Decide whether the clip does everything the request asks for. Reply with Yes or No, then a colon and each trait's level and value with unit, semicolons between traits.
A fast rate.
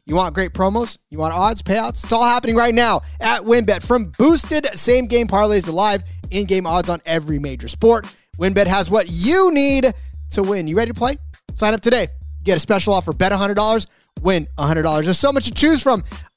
Yes: fast, 210 wpm